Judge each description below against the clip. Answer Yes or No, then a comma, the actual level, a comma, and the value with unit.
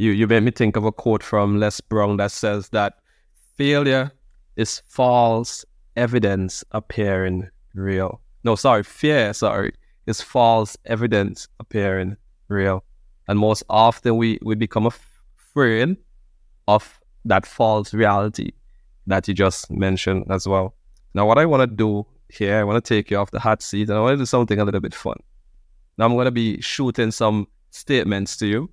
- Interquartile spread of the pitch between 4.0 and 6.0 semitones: No, average, 2.8 semitones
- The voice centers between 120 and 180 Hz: No, low, 105 Hz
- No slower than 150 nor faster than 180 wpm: Yes, average, 170 wpm